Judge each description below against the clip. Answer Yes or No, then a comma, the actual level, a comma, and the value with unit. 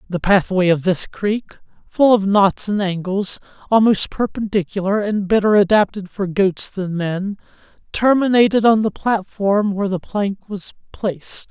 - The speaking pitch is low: No, high, 200 Hz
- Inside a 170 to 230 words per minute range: No, average, 145 wpm